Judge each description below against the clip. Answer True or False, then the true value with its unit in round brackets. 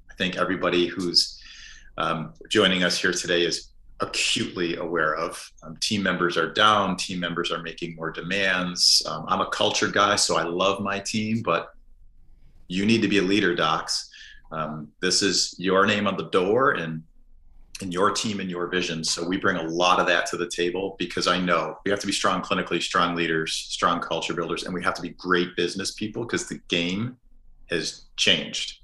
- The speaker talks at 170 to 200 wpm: True (195 wpm)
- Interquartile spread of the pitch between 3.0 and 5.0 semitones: False (2.5 semitones)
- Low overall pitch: True (90 Hz)